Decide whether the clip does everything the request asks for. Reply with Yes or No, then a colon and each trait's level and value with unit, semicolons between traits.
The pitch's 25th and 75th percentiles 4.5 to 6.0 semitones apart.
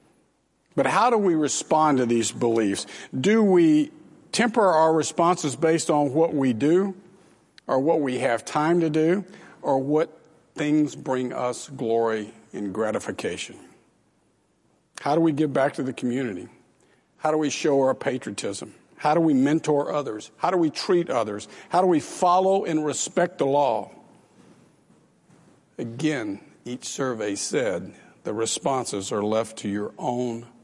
Yes: average, 5.3 semitones